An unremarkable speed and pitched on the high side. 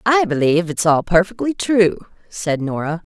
No: average, 155 wpm; medium, 180 Hz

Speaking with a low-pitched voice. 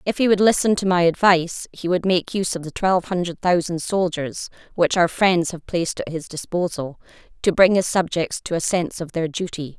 No: medium, 175 Hz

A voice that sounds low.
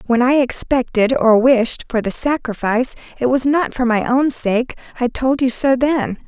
No: very high, 250 Hz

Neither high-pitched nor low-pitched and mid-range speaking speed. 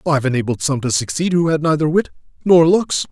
No: medium, 150 Hz; fast, 210 wpm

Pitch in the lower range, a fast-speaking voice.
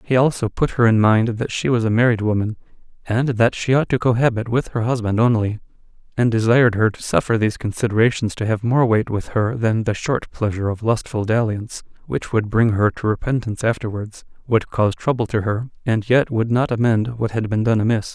Yes: low, 115 Hz; fast, 210 wpm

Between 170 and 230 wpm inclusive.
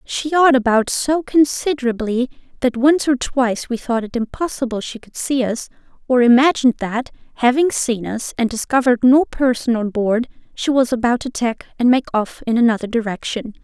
Yes: average, 175 wpm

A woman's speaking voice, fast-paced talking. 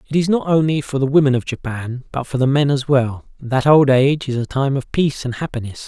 No: male; fast, 255 wpm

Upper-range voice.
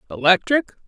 Yes: high, 195 Hz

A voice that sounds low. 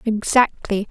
No: high, 215 Hz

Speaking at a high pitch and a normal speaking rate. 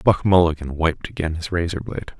No: very low, 85 Hz; average, 165 wpm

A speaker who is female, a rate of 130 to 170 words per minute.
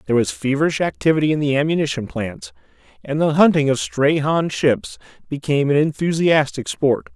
No: male; average, 160 wpm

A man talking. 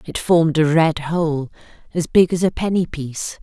No: female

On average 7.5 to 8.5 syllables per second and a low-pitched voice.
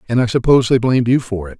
Yes: 7.8 syllables/s; low, 120 Hz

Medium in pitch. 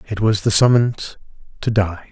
No: low, 105 Hz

